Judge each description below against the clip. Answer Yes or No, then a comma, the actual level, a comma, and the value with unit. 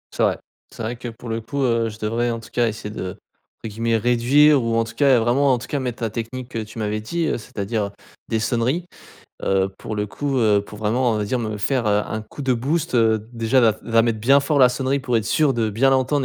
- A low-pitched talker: Yes, low, 115 Hz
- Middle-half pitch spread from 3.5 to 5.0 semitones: No, average, 3.0 semitones